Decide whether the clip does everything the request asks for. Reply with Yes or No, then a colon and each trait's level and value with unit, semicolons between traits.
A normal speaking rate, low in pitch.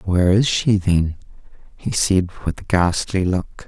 Yes: average, 165 wpm; very low, 95 Hz